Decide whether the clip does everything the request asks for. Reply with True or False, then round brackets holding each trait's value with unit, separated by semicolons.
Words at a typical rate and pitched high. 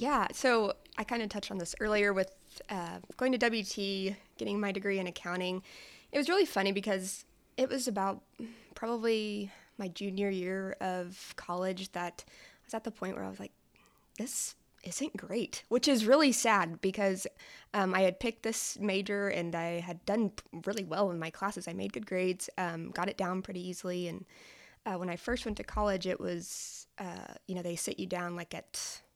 True (195 wpm; 195 Hz)